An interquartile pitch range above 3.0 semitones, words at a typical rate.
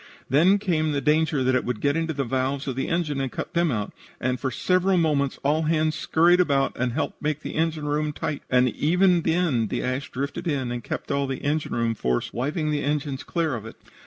No: average, 3.5 semitones; fast, 225 wpm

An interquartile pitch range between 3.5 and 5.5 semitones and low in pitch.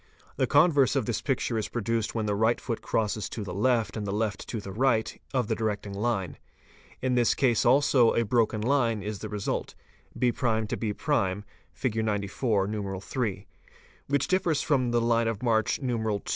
No: average, 3.0 semitones; low, 115 Hz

